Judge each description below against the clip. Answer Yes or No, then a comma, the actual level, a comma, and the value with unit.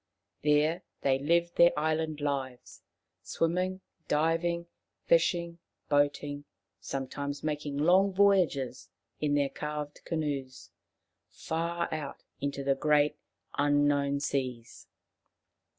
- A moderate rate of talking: No, slow, 95 wpm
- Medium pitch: Yes, medium, 150 Hz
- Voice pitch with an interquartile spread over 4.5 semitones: No, average, 2.8 semitones